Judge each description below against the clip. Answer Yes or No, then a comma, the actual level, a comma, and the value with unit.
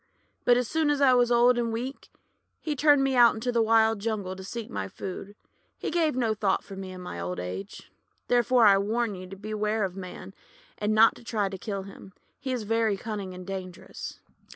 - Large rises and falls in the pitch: No, average, 3.9 semitones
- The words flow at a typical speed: No, fast, 215 wpm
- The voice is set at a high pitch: Yes, high, 215 Hz